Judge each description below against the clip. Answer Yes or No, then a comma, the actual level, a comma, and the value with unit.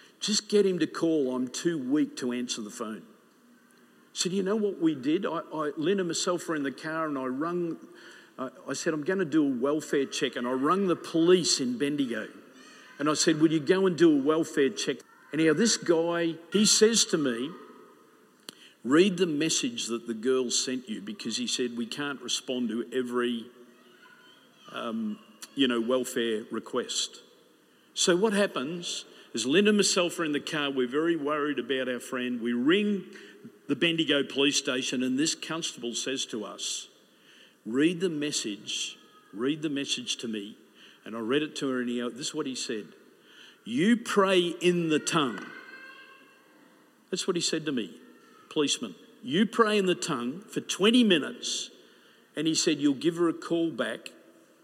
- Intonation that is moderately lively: No, wide, 8.0 semitones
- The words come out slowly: No, average, 185 wpm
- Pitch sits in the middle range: Yes, medium, 165 Hz